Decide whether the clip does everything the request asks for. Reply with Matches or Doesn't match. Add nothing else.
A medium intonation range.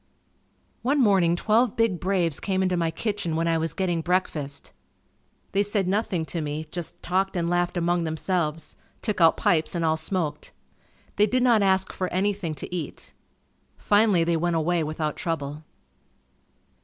Matches